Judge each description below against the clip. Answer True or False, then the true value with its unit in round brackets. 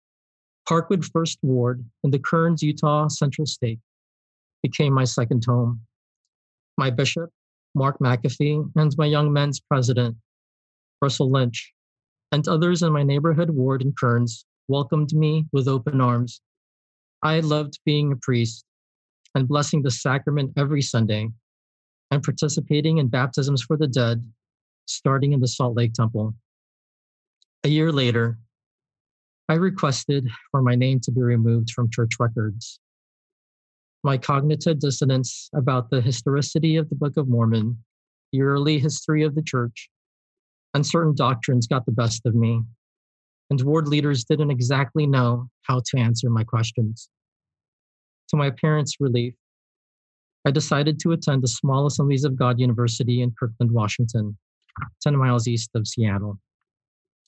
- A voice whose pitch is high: False (135 Hz)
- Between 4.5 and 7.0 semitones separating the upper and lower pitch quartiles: False (4.1 semitones)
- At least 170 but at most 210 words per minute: False (140 wpm)